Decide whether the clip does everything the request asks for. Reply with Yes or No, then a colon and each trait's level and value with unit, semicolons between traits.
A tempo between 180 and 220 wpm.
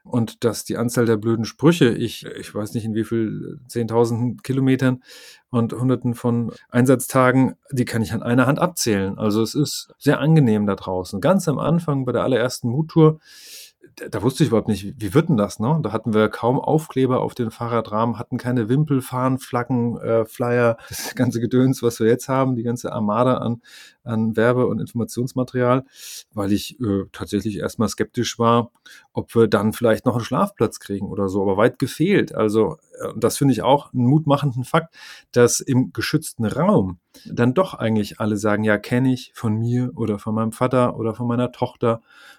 Yes: average, 185 wpm